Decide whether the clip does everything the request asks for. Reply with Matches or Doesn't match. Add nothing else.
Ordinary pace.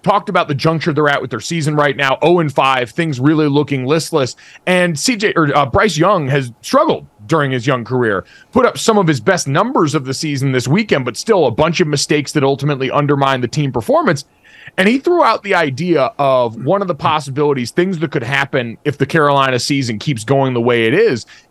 Doesn't match